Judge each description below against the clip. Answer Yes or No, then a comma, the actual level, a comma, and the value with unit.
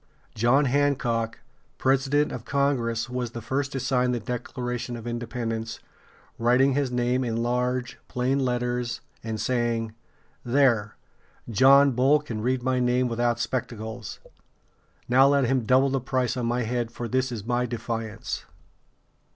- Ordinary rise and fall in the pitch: No, narrow, 1.9 semitones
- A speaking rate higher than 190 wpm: No, average, 145 wpm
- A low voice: Yes, low, 125 Hz